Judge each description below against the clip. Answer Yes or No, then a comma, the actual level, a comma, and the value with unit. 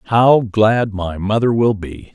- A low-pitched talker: Yes, low, 105 Hz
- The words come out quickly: No, average, 170 wpm